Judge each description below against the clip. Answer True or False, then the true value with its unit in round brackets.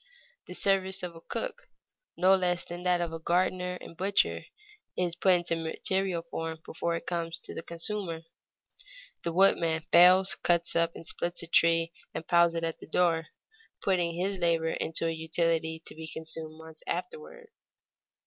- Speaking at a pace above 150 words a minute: True (160 wpm)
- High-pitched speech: False (170 Hz)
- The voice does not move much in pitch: True (1.7 semitones)